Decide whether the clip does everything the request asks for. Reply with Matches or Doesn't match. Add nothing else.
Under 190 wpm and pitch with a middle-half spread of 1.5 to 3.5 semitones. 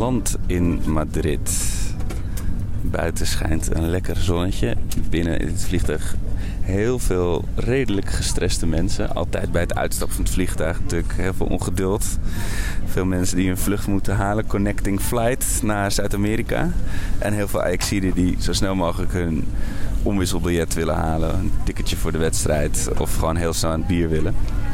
Matches